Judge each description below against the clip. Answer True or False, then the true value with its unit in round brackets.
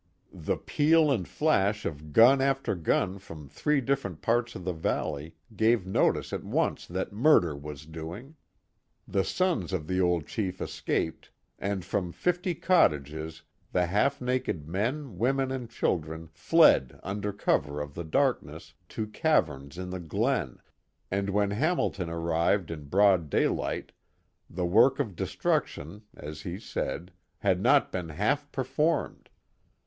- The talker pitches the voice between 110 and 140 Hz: False (95 Hz)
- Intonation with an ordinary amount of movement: False (7.4 semitones)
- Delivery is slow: False (145 wpm)